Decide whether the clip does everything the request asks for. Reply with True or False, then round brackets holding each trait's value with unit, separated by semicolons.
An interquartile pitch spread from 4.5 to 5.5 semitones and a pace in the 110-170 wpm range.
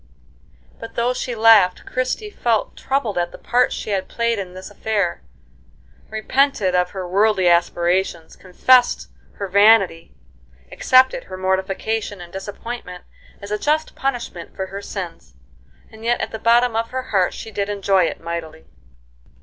False (4.1 semitones; 150 wpm)